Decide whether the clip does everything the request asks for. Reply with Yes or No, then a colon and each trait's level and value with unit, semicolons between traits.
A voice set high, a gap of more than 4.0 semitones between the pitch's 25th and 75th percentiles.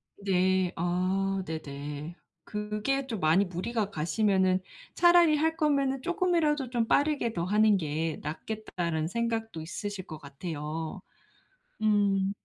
Yes: high, 195 Hz; wide, 5.6 semitones